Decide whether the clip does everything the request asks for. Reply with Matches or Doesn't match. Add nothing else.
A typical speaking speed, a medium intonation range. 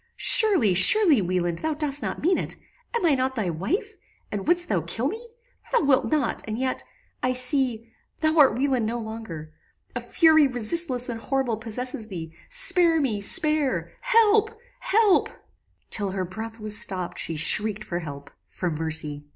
Doesn't match